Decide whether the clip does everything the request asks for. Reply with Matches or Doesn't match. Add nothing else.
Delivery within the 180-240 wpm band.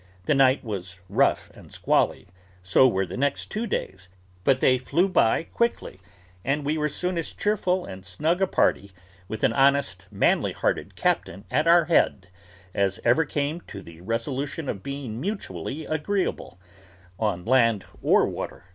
Doesn't match